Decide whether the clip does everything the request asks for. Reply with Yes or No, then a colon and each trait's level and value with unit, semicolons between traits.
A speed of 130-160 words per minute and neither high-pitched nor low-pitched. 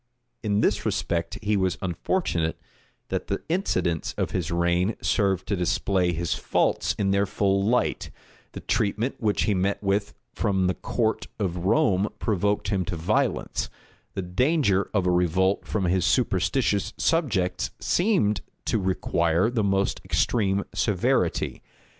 No: average, 140 wpm; low, 100 Hz